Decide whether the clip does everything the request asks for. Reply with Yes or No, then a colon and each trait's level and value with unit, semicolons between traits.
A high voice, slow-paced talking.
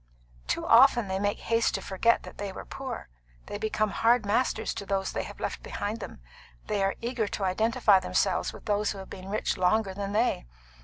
No: high, 205 Hz; fast, 205 wpm